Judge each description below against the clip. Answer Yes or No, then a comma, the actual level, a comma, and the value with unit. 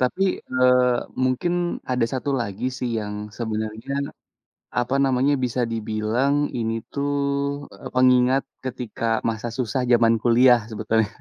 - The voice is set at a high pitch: No, low, 125 Hz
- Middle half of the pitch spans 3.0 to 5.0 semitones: No, narrow, 2.4 semitones